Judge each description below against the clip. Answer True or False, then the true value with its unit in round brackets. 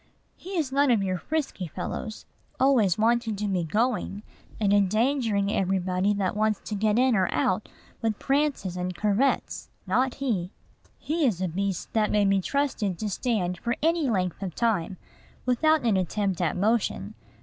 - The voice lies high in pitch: True (210 Hz)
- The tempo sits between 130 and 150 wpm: False (165 wpm)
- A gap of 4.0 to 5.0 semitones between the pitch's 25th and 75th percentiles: True (4.7 semitones)